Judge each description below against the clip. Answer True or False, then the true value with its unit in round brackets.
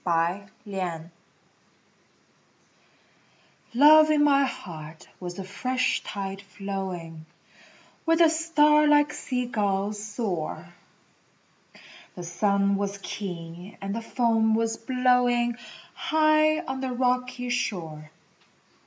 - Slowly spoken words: True (95 wpm)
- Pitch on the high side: True (215 Hz)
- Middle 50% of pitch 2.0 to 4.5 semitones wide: False (5.5 semitones)